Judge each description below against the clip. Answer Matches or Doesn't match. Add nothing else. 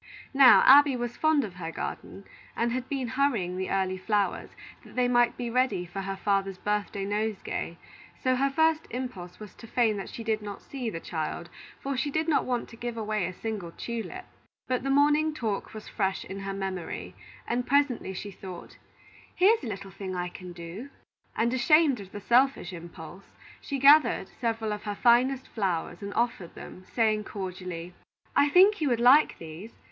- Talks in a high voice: Matches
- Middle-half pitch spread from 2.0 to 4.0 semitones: Doesn't match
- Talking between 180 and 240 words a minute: Matches